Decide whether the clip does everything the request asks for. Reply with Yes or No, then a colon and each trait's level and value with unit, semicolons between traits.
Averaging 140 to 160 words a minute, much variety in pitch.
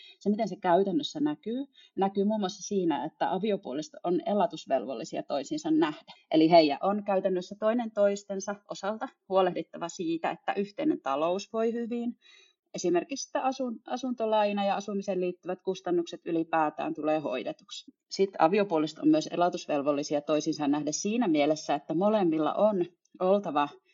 No: average, 130 wpm; wide, 6.7 semitones